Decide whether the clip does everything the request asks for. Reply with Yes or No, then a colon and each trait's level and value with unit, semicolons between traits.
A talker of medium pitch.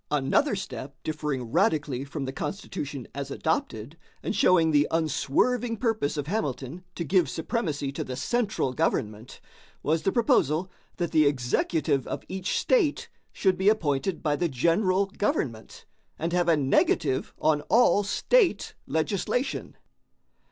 Yes: medium, 160 Hz